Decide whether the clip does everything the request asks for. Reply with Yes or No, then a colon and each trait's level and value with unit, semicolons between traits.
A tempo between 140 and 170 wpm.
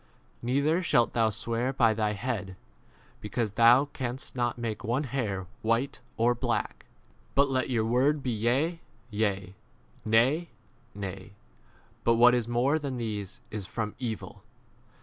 Yes: average, 145 wpm